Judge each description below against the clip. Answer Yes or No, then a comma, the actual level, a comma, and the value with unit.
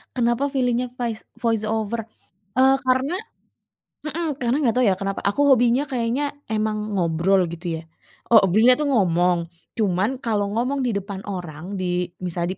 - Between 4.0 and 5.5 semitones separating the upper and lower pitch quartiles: Yes, average, 5.2 semitones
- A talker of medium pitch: No, high, 220 Hz